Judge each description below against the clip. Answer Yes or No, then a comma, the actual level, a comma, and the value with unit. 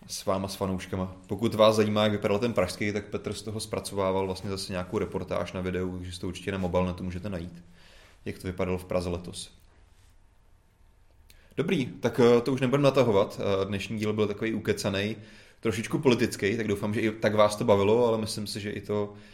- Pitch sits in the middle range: No, low, 100 Hz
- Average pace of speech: No, fast, 195 wpm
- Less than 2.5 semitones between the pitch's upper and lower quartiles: No, average, 2.8 semitones